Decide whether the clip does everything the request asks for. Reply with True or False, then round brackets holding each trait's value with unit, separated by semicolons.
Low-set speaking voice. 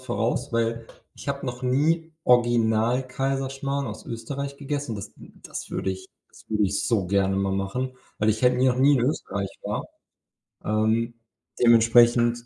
True (120 Hz)